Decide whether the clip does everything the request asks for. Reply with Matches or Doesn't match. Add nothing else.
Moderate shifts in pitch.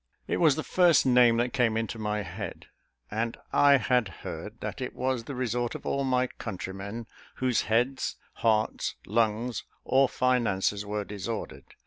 Matches